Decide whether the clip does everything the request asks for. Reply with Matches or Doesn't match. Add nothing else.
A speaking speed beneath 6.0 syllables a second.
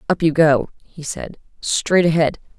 Matches